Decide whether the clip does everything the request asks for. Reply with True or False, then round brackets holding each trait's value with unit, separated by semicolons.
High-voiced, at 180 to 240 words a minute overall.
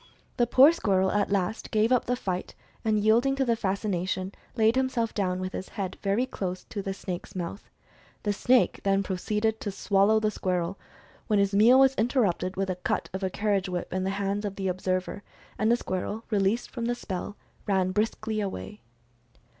True (200 Hz; 190 wpm)